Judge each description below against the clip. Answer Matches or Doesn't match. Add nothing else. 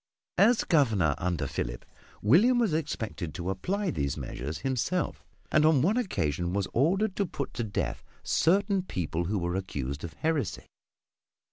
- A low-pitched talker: Matches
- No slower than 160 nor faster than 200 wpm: Doesn't match